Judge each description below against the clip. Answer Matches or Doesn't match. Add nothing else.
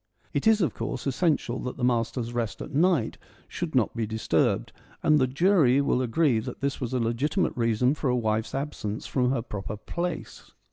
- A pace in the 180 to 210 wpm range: Matches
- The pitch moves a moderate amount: Matches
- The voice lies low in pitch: Matches